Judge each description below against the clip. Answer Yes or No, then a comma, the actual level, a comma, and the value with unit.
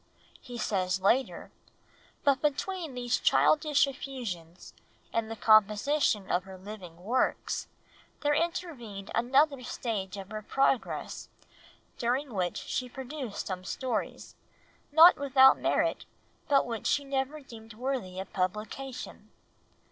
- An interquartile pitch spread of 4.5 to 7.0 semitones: Yes, average, 5.3 semitones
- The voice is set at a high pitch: Yes, high, 245 Hz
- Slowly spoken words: Yes, slow, 120 wpm